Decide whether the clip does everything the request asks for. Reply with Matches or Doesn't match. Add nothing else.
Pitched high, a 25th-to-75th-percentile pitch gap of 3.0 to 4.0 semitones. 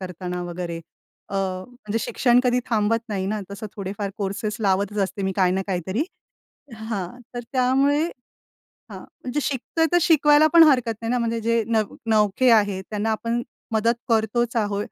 Matches